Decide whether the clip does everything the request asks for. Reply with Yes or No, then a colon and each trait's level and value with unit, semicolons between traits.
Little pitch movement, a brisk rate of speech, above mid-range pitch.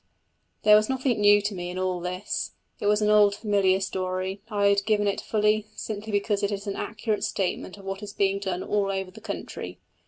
Yes: narrow, 1.5 semitones; fast, 215 wpm; high, 200 Hz